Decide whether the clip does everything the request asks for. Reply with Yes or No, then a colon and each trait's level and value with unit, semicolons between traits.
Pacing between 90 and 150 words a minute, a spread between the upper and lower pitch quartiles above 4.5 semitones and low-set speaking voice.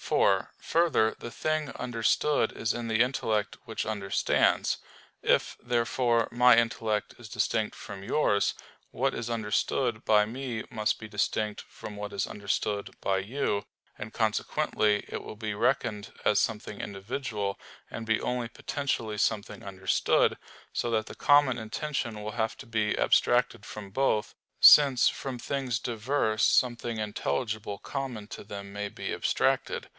No: average, 145 wpm; narrow, 2.6 semitones; low, 110 Hz